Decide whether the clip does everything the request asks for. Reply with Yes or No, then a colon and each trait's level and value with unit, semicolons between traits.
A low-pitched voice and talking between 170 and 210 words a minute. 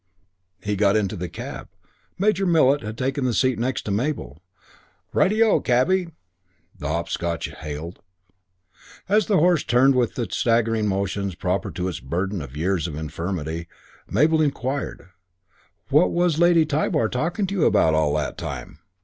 No: low, 115 Hz; average, 155 wpm